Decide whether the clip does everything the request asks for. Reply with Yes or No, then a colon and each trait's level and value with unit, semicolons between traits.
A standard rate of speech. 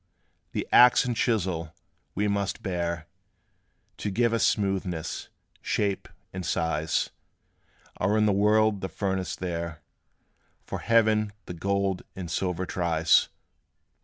No: slow, 120 wpm